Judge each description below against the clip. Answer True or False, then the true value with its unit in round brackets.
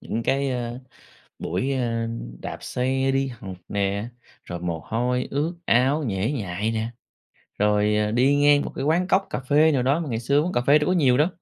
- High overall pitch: False (125 Hz)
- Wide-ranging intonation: False (4.7 semitones)